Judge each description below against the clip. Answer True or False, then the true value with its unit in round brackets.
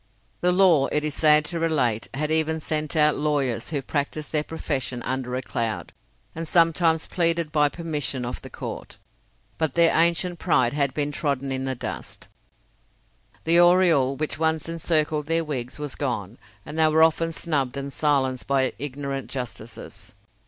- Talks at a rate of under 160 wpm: False (165 wpm)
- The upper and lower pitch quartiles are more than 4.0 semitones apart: False (3.3 semitones)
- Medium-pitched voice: True (150 Hz)